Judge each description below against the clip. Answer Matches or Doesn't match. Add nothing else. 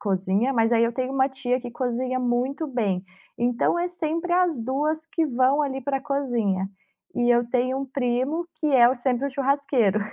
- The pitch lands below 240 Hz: Doesn't match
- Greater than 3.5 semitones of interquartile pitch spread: Doesn't match